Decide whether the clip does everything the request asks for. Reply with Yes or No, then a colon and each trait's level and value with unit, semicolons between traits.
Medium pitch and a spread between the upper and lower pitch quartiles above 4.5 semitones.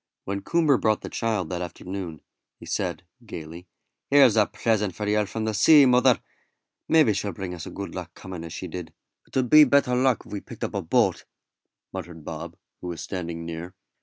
No: low, 100 Hz; average, 5.2 semitones